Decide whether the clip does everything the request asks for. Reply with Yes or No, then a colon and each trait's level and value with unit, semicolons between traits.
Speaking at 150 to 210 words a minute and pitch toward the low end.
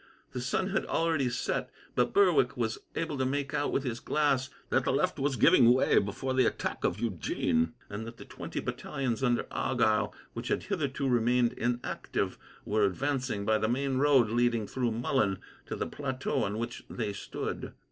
Yes: average, 180 wpm; low, 125 Hz